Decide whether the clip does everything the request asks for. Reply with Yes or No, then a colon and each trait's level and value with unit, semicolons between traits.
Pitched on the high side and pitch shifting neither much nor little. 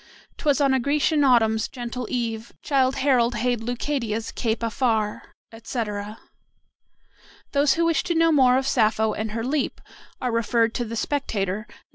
Yes: high, 240 Hz; average, 3.6 semitones